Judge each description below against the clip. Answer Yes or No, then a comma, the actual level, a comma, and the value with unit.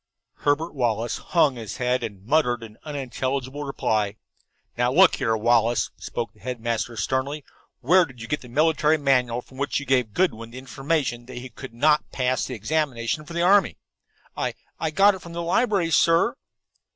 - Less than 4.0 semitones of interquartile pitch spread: No, average, 4.5 semitones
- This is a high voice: No, low, 130 Hz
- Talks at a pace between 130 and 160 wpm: No, average, 175 wpm